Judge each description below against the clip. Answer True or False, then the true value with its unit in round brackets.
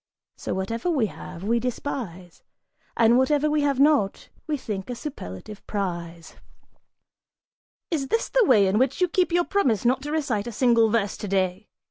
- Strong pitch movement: True (6.6 semitones)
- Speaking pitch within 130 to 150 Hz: False (235 Hz)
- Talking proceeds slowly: False (165 wpm)